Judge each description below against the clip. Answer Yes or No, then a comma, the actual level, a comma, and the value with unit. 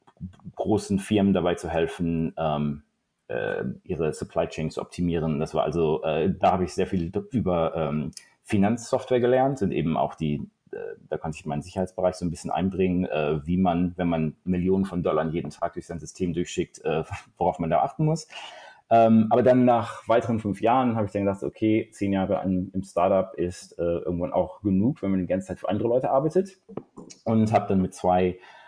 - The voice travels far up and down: No, average, 4.3 semitones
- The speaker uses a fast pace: Yes, fast, 200 wpm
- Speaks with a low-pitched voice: Yes, very low, 95 Hz